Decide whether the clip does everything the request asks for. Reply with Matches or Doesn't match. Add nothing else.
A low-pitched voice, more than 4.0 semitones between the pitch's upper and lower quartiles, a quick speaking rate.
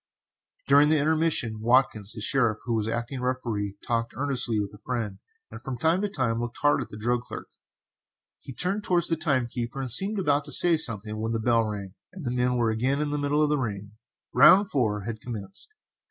Matches